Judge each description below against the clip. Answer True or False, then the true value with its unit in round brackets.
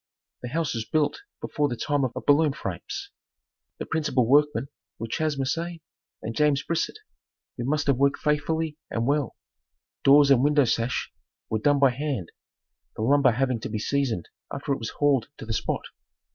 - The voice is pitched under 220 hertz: True (140 Hz)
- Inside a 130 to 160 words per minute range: False (175 wpm)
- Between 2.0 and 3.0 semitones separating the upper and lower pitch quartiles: False (3.4 semitones)